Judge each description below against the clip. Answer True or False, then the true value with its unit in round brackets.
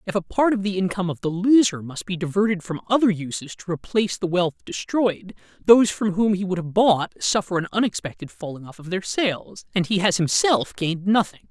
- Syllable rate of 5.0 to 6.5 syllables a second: True (5.6 syllables/s)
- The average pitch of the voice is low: False (190 Hz)